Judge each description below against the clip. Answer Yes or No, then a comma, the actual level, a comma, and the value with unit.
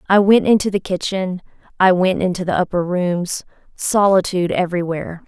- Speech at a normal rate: Yes, average, 150 wpm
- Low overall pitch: No, medium, 185 Hz